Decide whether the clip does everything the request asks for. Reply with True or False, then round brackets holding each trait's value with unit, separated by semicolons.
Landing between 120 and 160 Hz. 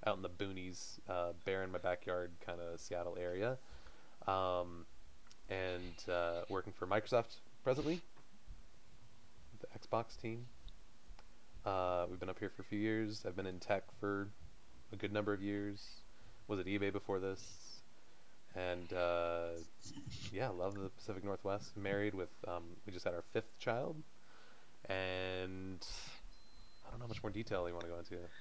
False (95 Hz)